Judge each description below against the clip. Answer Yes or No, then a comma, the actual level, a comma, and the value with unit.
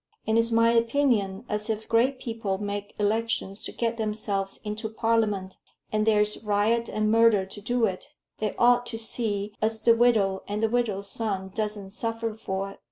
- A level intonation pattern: Yes, narrow, 2.1 semitones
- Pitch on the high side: Yes, high, 215 Hz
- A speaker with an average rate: Yes, average, 175 wpm